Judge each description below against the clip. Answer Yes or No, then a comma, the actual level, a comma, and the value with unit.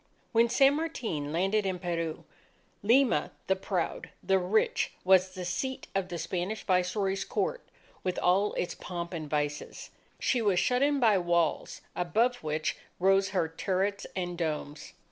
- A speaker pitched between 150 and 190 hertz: Yes, medium, 185 Hz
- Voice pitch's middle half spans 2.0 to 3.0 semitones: No, average, 3.5 semitones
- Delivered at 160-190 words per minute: No, average, 150 wpm